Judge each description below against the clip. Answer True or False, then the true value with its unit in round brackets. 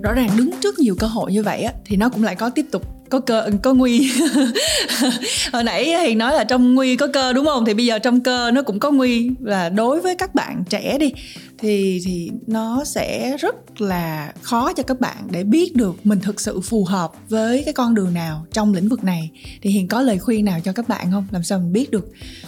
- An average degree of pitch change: True (4.4 semitones)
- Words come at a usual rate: True (240 wpm)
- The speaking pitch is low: False (225 Hz)